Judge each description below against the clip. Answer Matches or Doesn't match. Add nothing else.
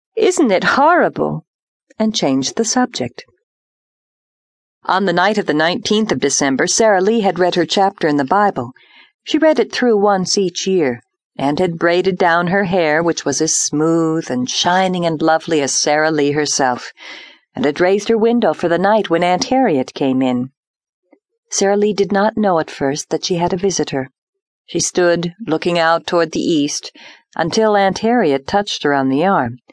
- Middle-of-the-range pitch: Matches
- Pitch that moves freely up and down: Matches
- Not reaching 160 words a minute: Doesn't match